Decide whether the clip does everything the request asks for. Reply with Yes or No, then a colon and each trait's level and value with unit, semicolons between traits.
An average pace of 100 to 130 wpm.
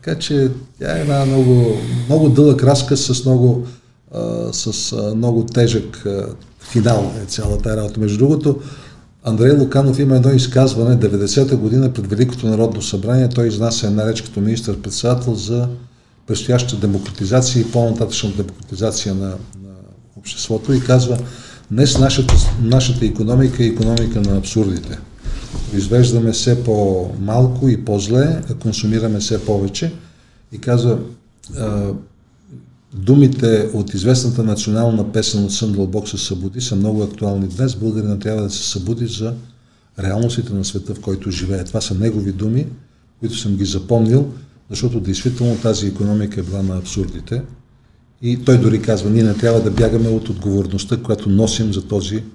No: average, 145 wpm